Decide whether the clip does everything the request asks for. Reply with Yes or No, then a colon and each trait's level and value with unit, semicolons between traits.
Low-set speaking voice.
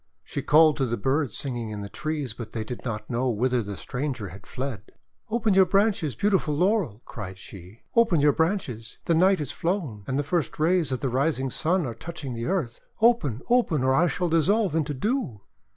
No: medium, 145 Hz